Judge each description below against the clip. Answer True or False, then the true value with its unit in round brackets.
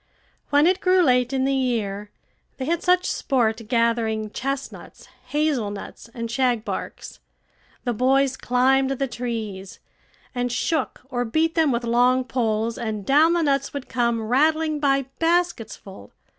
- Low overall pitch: False (255 Hz)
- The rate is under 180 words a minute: True (145 wpm)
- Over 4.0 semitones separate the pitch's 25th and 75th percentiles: False (3.5 semitones)